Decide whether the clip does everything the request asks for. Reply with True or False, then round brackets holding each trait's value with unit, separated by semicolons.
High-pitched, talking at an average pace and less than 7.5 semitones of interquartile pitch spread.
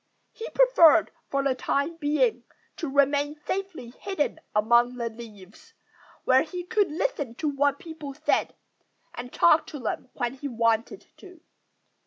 True (285 Hz; 145 wpm; 5.4 semitones)